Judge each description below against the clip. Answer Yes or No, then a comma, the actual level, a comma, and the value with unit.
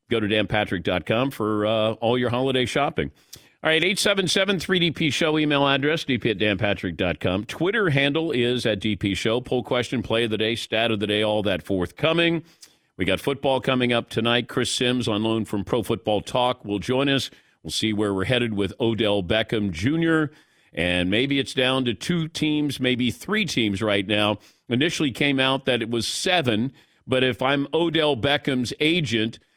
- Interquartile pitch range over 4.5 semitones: Yes, average, 5.1 semitones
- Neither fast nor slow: Yes, average, 180 wpm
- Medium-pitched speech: No, low, 125 Hz